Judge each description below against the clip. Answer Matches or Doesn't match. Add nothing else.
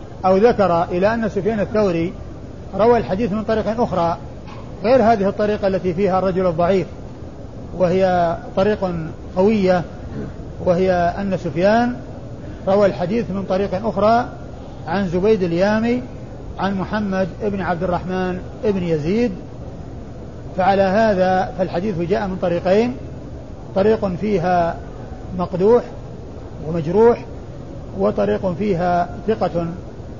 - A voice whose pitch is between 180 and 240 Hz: Matches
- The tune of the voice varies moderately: Matches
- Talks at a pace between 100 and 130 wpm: Matches